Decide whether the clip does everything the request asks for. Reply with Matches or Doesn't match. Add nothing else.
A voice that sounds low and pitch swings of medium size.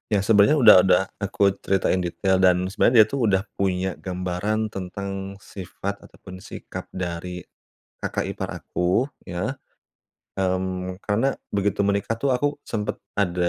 Doesn't match